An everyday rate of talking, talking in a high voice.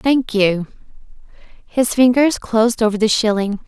No: slow, 130 wpm; high, 225 Hz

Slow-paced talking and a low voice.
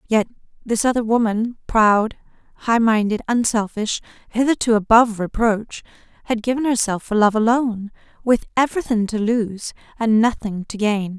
No: slow, 130 wpm; high, 225 Hz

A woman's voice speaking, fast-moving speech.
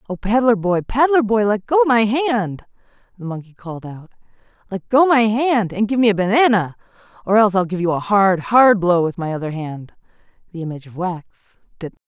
Yes: female; fast, 215 wpm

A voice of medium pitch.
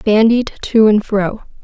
No: high, 215 Hz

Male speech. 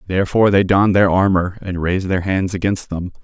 Yes: male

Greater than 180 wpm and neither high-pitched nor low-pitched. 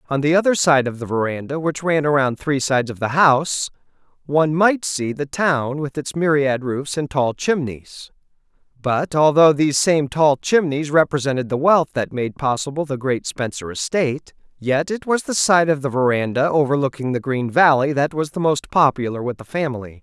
Yes: average, 190 wpm; medium, 145 Hz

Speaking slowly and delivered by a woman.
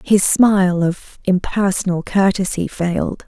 Yes: slow, 110 wpm; female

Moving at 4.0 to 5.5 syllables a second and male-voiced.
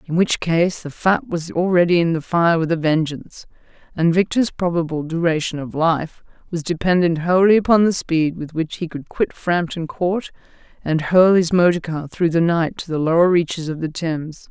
No: 5.0 syllables/s; female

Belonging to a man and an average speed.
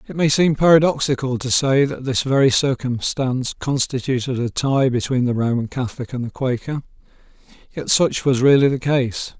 Yes: male; average, 165 wpm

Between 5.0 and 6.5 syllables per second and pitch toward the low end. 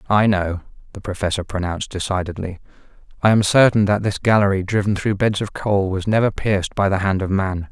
Yes: 5.8 syllables/s; low, 100 Hz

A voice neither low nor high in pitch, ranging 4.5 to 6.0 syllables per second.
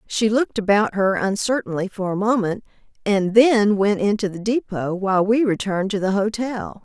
No: high, 205 Hz; 5.1 syllables/s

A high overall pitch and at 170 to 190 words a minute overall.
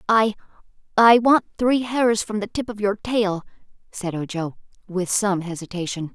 No: high, 205 Hz; average, 145 wpm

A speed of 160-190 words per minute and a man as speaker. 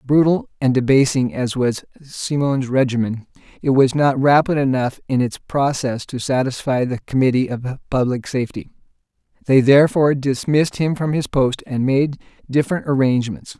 No: average, 145 wpm; male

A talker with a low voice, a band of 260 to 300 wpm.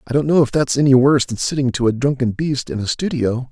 Yes: low, 130 Hz; fast, 275 wpm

